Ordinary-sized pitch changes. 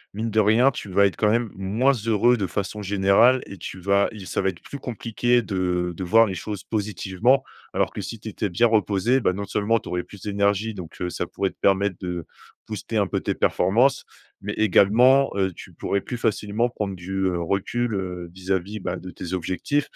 Yes: average, 3.2 semitones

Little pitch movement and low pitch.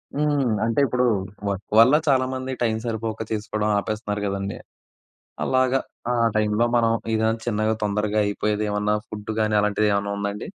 Yes: narrow, 2.2 semitones; low, 110 Hz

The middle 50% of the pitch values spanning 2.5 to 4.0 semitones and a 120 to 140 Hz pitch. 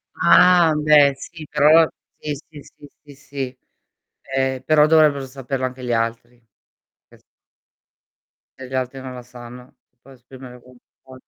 Yes: average, 2.9 semitones; low, 135 Hz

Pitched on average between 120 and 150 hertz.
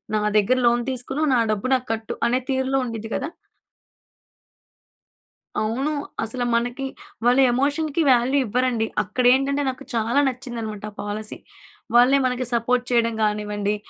No: high, 245 Hz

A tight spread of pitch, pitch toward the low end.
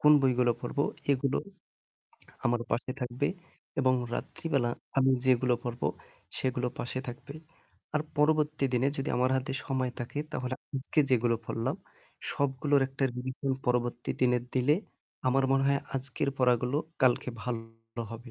Yes: narrow, 1.9 semitones; low, 130 Hz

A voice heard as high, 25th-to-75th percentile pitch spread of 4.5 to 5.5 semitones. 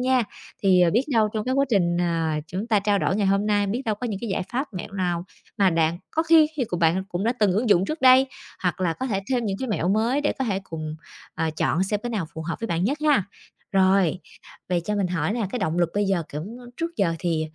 Yes: high, 200 Hz; average, 5.0 semitones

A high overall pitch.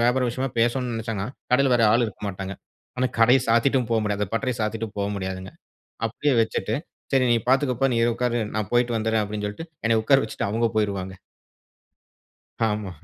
No: low, 115 Hz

